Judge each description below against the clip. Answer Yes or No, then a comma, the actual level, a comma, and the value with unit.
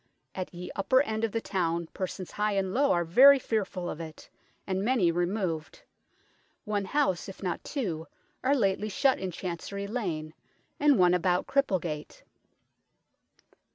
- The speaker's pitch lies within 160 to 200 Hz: Yes, high, 190 Hz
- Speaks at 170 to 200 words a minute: No, average, 150 wpm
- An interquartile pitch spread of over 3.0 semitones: Yes, average, 4.2 semitones